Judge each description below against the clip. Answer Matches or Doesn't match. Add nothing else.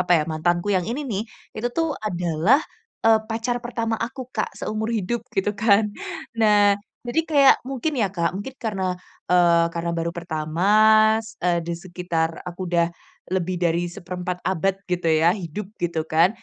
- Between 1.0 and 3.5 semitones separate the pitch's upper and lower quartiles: Doesn't match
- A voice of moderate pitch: Matches